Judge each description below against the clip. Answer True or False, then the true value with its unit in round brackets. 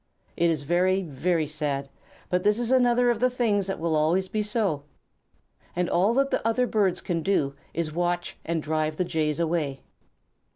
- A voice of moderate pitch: True (175 Hz)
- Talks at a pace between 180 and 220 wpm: True (190 wpm)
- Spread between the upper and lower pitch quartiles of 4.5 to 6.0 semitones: True (5.2 semitones)